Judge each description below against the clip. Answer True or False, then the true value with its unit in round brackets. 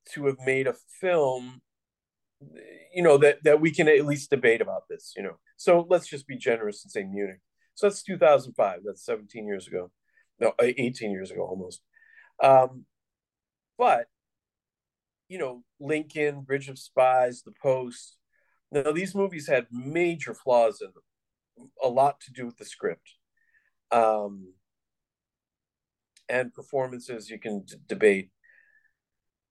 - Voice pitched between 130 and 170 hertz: True (140 Hz)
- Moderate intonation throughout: False (8.2 semitones)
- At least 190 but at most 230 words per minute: False (140 wpm)